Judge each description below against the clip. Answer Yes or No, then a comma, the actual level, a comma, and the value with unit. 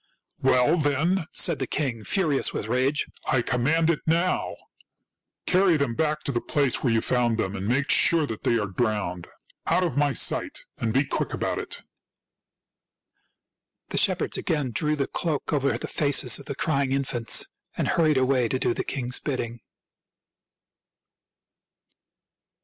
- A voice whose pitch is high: No, low, 135 Hz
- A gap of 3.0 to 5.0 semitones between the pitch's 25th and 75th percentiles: Yes, average, 4.1 semitones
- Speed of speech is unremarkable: Yes, average, 160 wpm